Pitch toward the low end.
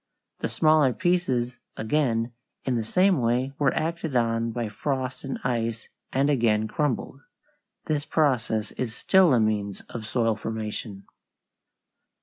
Yes: low, 125 Hz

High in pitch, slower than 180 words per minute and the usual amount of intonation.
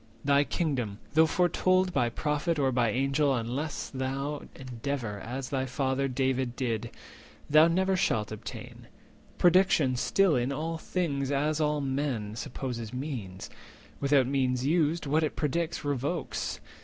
No: medium, 140 Hz; slow, 135 wpm; average, 3.5 semitones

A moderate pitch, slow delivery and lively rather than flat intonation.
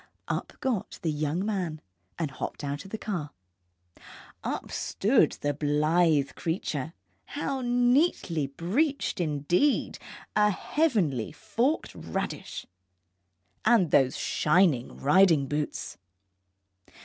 Yes: medium, 170 Hz; slow, 100 wpm; wide, 6.8 semitones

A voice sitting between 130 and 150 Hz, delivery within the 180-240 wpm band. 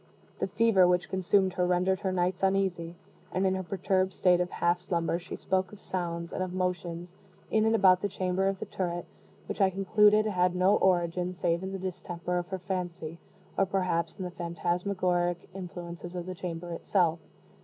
No: medium, 180 Hz; average, 185 wpm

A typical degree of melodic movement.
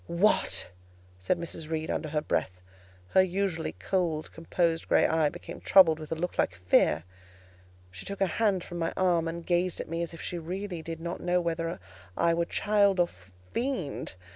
No: narrow, 2.2 semitones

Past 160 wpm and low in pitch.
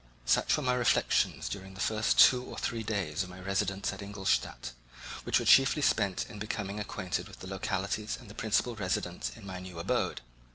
Yes: average, 195 wpm; low, 100 Hz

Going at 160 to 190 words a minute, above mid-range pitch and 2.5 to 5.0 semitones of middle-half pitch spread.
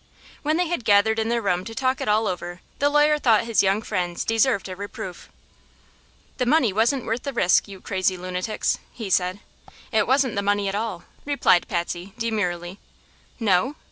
Yes: average, 180 wpm; high, 210 Hz; average, 4.3 semitones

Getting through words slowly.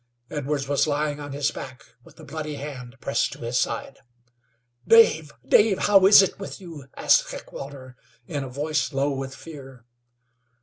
No: average, 165 wpm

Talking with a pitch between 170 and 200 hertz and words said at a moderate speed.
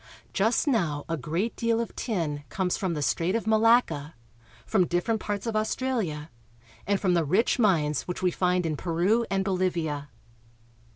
Yes: medium, 185 Hz; average, 165 wpm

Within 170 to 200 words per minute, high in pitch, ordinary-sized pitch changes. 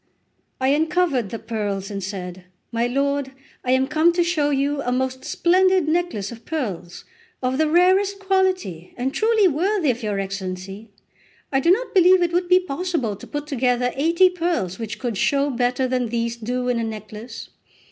No: average, 180 wpm; very high, 265 Hz; wide, 7.4 semitones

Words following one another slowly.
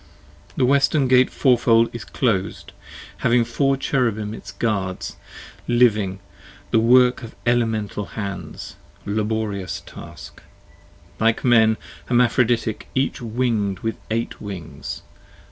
Yes: slow, 105 wpm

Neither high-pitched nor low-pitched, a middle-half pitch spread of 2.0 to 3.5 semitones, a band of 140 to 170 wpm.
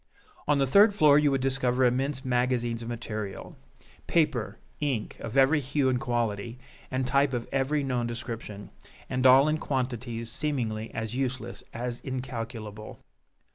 No: low, 125 Hz; narrow, 2.6 semitones; average, 145 wpm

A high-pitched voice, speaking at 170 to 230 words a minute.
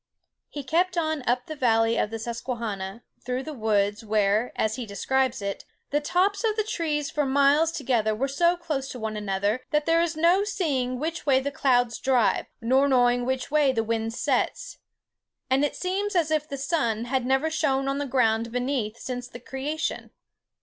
Yes: very high, 265 Hz; average, 185 wpm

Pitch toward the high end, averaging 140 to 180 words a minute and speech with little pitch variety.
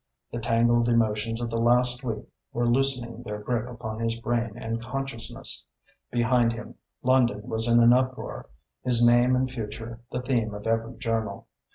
No: low, 120 Hz; average, 165 wpm; narrow, 1.4 semitones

